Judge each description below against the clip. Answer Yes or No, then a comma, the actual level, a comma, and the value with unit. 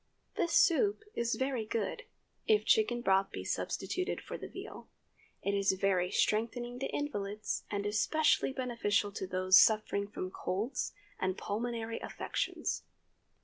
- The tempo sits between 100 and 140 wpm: Yes, slow, 135 wpm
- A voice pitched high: Yes, high, 220 Hz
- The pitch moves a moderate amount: Yes, average, 4.4 semitones